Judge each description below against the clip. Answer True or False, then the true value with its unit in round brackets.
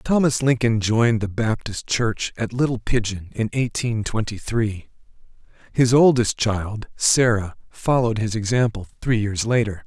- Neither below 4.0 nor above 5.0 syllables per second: True (4.5 syllables/s)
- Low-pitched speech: True (115 Hz)